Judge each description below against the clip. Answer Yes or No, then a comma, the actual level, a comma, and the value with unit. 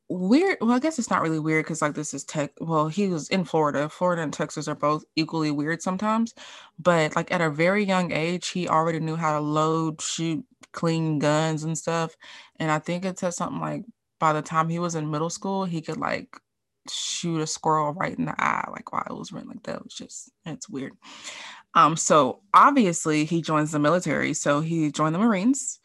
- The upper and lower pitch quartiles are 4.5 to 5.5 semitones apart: No, average, 3.0 semitones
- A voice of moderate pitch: Yes, medium, 160 Hz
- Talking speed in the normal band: No, fast, 220 wpm